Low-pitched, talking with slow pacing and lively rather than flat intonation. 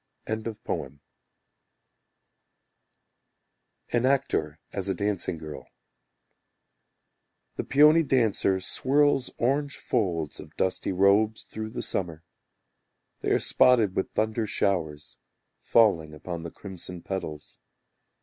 Yes: low, 100 Hz; slow, 95 wpm; wide, 5.7 semitones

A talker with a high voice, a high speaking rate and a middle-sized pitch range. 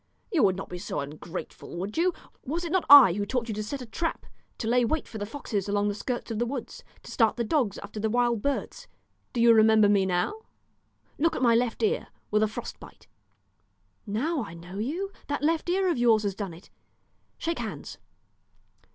No: high, 230 Hz; fast, 210 wpm; wide, 5.8 semitones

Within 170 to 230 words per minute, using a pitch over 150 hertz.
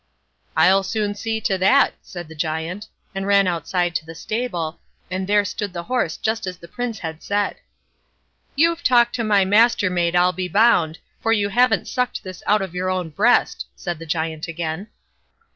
Yes: average, 180 wpm; high, 190 Hz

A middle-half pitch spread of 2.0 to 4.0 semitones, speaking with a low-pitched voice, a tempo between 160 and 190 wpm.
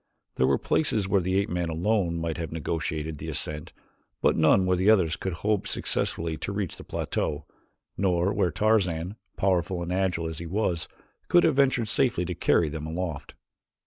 Yes: average, 3.4 semitones; very low, 90 Hz; average, 180 wpm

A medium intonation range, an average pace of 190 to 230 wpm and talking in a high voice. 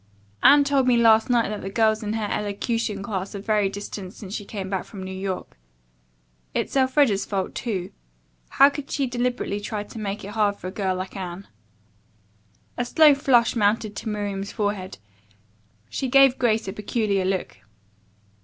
No: average, 3.4 semitones; average, 170 wpm; high, 210 Hz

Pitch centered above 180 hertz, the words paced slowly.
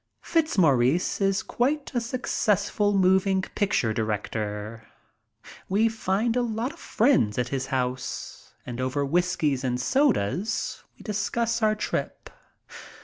Yes: high, 190 Hz; slow, 120 wpm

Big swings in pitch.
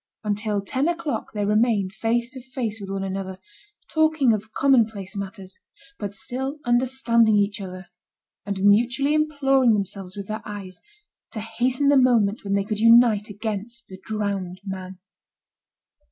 No: average, 3.8 semitones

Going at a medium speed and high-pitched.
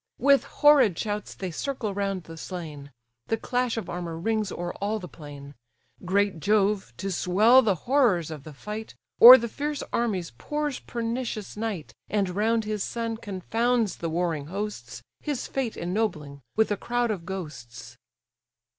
Yes: average, 155 wpm; high, 205 Hz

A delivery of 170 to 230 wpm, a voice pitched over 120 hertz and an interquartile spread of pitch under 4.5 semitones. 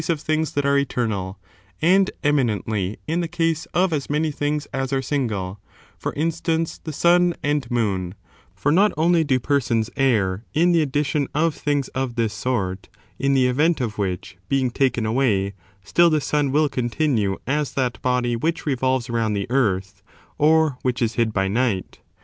No: average, 175 wpm; low, 135 Hz; average, 5.3 semitones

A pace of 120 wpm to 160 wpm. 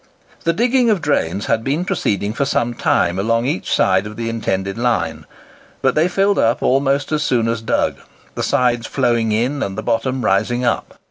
No: average, 190 wpm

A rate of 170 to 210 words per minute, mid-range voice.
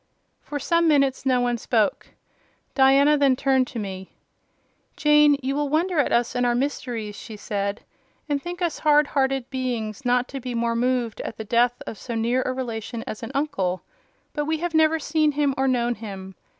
No: average, 190 wpm; very high, 255 Hz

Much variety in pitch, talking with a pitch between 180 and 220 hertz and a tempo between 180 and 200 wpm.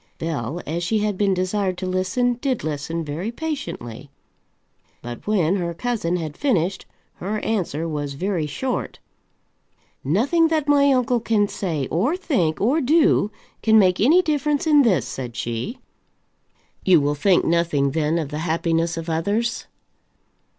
No: wide, 7.0 semitones; medium, 185 Hz; average, 150 wpm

